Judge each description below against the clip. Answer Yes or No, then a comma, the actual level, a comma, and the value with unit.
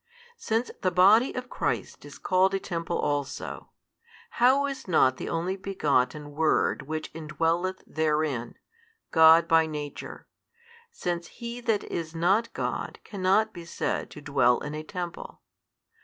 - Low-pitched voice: No, medium, 170 Hz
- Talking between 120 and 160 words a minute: Yes, average, 140 wpm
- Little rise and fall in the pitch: No, average, 4.2 semitones